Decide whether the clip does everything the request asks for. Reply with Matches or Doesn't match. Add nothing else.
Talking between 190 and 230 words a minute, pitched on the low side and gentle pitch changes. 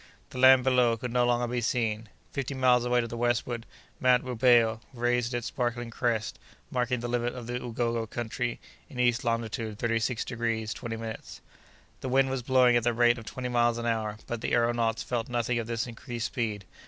Matches